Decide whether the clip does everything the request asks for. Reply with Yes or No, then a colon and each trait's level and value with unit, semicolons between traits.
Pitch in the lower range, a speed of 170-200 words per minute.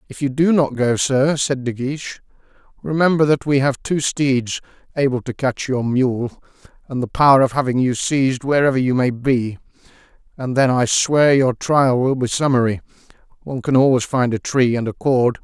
Yes: low, 130 Hz; average, 190 wpm